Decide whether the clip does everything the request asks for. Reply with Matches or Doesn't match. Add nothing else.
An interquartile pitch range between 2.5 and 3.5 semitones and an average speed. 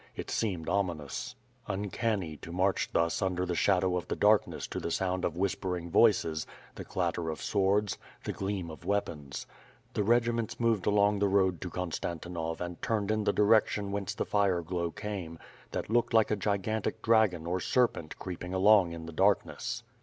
Matches